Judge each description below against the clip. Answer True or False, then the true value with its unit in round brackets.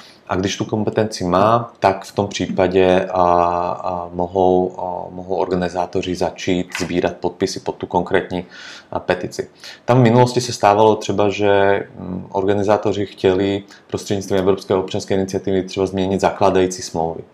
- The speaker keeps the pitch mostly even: True (1.9 semitones)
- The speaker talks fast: False (140 wpm)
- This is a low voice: True (95 Hz)